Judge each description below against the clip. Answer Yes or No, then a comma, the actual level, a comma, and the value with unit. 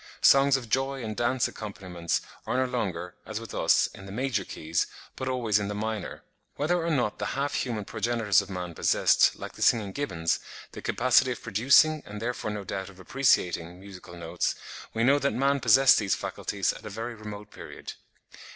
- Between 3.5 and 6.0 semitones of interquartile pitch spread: Yes, average, 4.9 semitones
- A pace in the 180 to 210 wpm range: Yes, average, 190 wpm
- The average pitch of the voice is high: No, low, 110 Hz